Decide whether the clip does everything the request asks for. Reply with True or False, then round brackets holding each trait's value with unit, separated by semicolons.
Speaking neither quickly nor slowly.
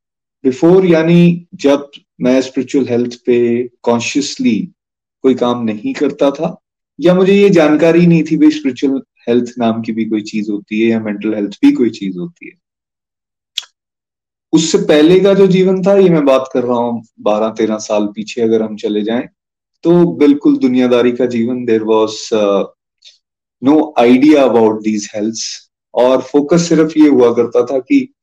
True (160 wpm)